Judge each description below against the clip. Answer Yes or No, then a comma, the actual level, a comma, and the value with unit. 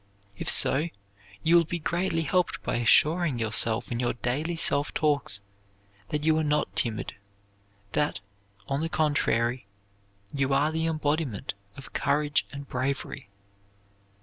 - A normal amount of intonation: Yes, average, 3.9 semitones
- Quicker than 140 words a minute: No, slow, 135 wpm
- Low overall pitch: No, medium, 145 Hz